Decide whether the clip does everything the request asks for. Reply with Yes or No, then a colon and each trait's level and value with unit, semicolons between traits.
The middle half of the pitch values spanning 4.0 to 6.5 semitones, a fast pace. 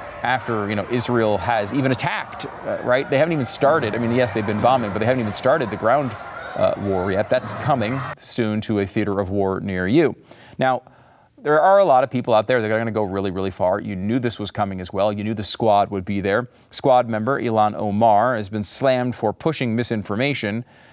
No: average, 3.2 semitones; fast, 230 wpm